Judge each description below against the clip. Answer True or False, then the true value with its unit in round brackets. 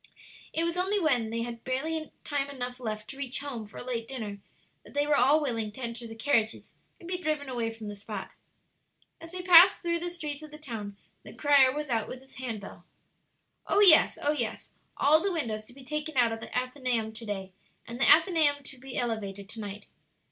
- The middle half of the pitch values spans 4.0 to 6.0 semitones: True (5.1 semitones)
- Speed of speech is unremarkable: False (220 wpm)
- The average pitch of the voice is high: True (260 Hz)